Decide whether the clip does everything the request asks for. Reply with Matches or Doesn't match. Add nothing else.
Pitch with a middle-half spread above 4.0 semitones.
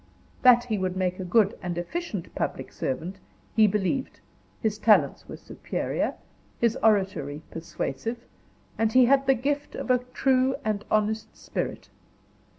Matches